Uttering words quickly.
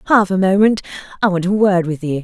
Yes: fast, 240 wpm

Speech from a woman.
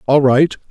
No: male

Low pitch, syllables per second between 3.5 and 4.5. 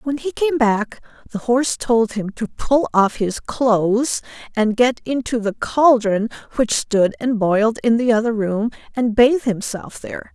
No: high, 230 Hz; 4.3 syllables/s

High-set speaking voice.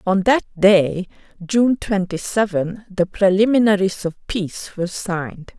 Yes: high, 195 Hz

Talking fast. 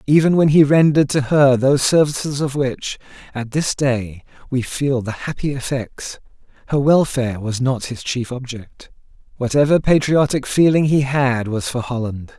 No: average, 160 wpm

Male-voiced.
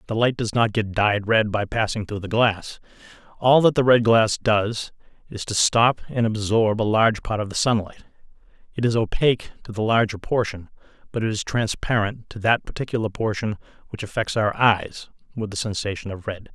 Yes: male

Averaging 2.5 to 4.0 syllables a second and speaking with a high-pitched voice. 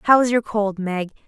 No: 4.7 syllables/s; high, 210 Hz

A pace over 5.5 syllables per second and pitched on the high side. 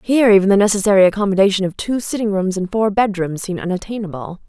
Yes: 6.9 syllables/s; high, 200 Hz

